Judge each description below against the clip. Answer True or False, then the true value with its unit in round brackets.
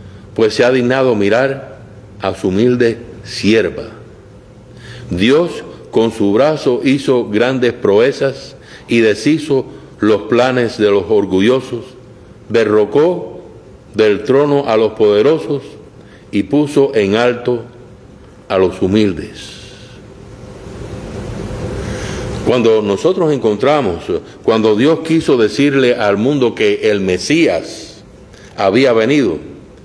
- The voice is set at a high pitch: False (115 Hz)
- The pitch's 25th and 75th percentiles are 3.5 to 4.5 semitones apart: True (4.2 semitones)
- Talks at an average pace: False (100 wpm)